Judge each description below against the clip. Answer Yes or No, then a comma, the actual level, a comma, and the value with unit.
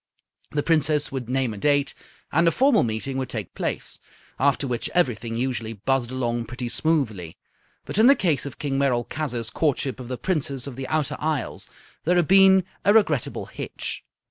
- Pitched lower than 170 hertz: Yes, low, 135 Hz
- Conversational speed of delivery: Yes, average, 175 wpm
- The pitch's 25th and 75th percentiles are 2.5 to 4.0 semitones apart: No, average, 4.6 semitones